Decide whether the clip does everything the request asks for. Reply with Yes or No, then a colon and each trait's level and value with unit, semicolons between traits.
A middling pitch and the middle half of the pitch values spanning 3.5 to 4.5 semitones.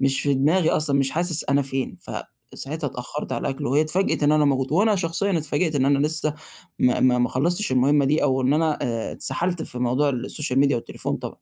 No: medium, 145 Hz; average, 3.0 semitones